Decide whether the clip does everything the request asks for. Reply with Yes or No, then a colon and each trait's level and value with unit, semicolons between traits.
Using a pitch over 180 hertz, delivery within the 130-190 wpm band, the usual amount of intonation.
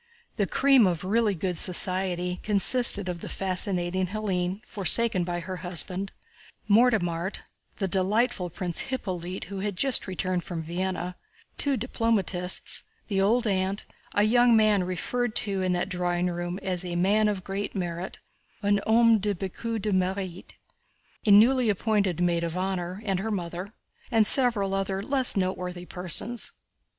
Yes: high, 190 Hz; average, 150 wpm; average, 3.0 semitones